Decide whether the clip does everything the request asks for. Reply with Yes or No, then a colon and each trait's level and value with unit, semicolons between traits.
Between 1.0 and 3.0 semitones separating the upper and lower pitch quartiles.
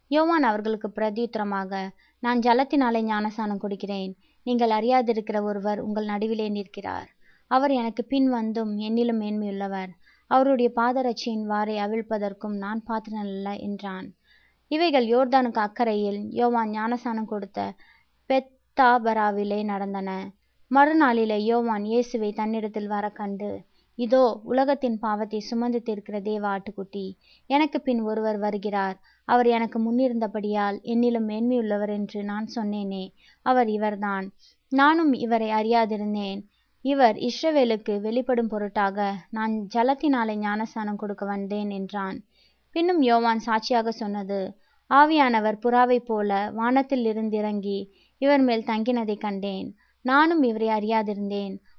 Yes: average, 2.7 semitones